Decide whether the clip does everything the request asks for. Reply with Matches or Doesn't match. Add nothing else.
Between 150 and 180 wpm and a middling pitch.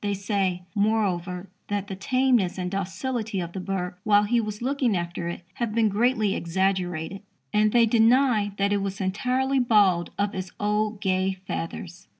Doesn't match